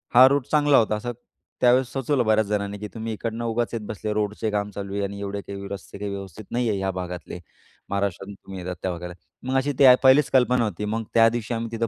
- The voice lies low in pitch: Yes, low, 105 Hz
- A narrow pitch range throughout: No, average, 3.2 semitones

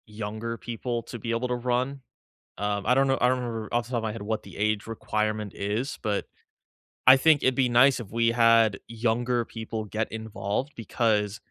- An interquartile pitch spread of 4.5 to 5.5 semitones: No, narrow, 2.4 semitones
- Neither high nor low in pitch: No, low, 115 Hz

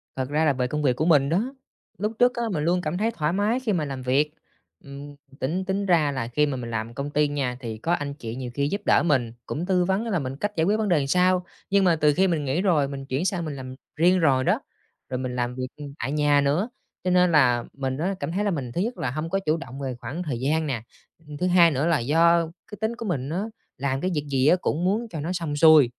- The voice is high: No, medium, 150 Hz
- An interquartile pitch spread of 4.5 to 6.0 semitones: Yes, average, 4.9 semitones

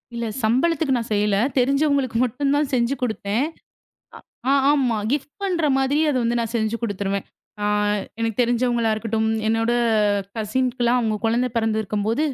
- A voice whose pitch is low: No, high, 235 Hz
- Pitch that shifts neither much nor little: Yes, average, 3.3 semitones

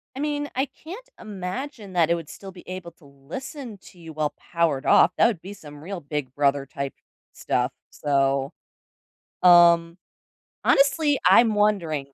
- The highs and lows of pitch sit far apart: Yes, wide, 6.7 semitones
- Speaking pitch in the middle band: Yes, medium, 175 Hz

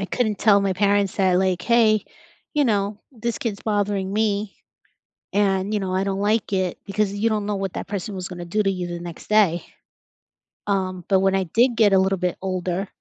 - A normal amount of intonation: No, narrow, 2.1 semitones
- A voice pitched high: Yes, high, 195 Hz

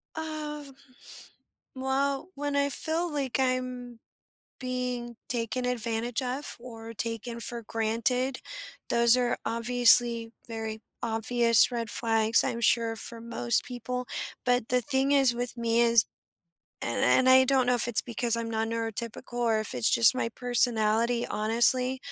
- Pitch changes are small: Yes, narrow, 1.8 semitones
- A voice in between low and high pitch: No, high, 240 Hz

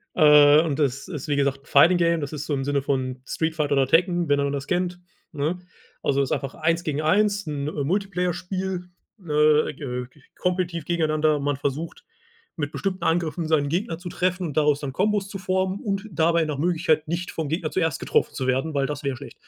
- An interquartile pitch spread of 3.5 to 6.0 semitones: Yes, average, 3.8 semitones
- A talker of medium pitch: Yes, medium, 155 Hz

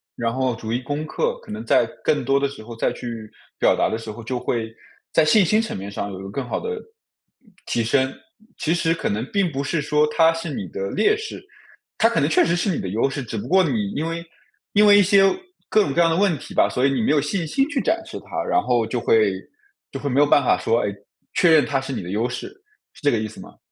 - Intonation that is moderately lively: No, wide, 6.7 semitones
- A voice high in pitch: No, medium, 140 Hz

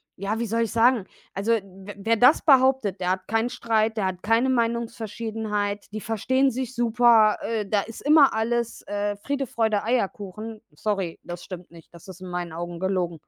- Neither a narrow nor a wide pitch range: Yes, average, 3.3 semitones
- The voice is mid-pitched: No, high, 220 Hz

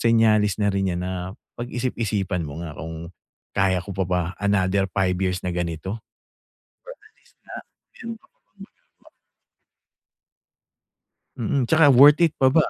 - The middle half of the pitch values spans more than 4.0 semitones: Yes, average, 5.2 semitones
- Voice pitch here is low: Yes, low, 100 Hz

